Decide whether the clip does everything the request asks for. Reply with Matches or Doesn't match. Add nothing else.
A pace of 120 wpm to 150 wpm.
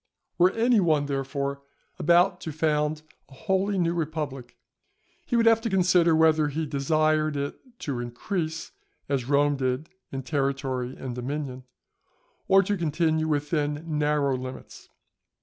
Matches